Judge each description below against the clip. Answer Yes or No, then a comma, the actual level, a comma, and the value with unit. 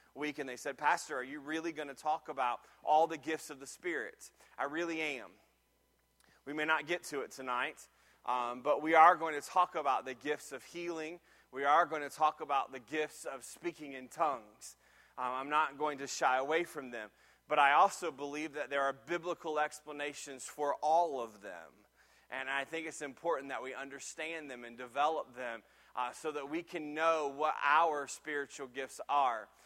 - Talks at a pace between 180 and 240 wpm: Yes, average, 195 wpm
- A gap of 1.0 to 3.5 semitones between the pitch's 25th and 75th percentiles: Yes, average, 2.8 semitones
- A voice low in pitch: No, medium, 150 Hz